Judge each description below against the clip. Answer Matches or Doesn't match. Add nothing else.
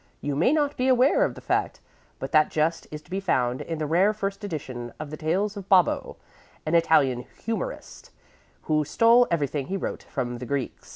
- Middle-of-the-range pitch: Matches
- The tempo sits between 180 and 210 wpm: Matches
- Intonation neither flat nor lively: Doesn't match